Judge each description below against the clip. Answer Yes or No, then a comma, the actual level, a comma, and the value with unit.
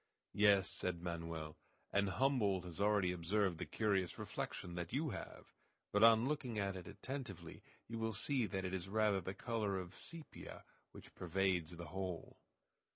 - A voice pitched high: No, very low, 95 Hz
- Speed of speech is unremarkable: Yes, average, 160 wpm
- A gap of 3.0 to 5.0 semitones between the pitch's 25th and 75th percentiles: Yes, average, 3.6 semitones